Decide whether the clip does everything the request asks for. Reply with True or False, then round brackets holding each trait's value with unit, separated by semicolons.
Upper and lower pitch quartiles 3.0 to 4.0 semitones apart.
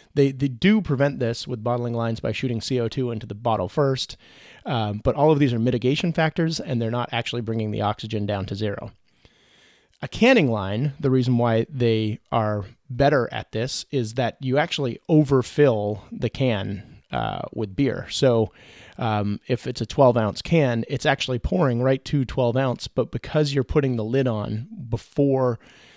True (3.7 semitones)